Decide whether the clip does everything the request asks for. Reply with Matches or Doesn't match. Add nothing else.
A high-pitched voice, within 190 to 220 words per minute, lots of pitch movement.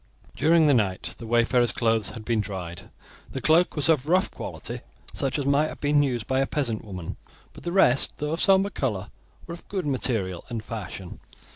Doesn't match